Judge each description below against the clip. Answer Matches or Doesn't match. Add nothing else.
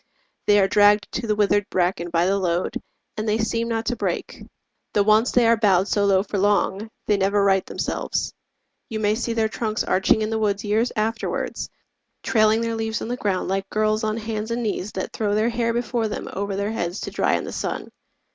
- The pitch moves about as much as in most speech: Doesn't match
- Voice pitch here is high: Matches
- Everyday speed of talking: Doesn't match